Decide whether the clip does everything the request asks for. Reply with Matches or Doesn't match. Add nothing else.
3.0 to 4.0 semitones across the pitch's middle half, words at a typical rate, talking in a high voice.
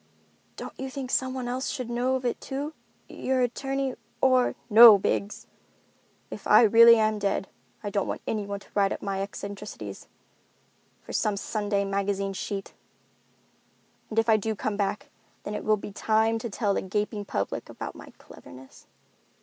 Matches